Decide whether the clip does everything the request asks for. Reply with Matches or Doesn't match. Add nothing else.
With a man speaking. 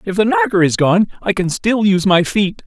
Matches